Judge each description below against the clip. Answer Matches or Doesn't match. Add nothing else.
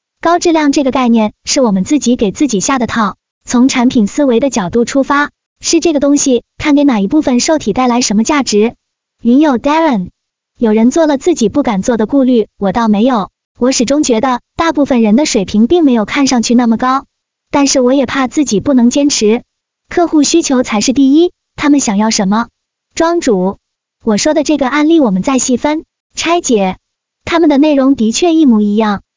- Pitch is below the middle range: Doesn't match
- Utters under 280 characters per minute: Doesn't match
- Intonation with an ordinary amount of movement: Matches